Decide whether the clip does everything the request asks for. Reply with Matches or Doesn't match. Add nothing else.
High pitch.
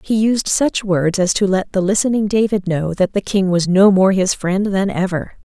Matches